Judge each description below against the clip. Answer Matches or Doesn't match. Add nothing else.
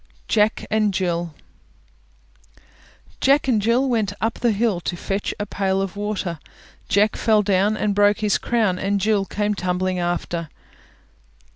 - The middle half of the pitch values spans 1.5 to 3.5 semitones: Matches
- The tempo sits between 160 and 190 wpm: Doesn't match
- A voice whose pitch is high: Matches